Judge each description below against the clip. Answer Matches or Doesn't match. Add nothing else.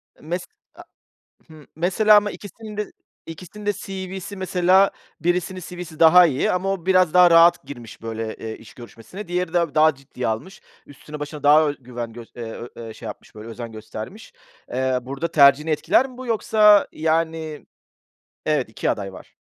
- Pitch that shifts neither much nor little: Doesn't match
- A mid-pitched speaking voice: Matches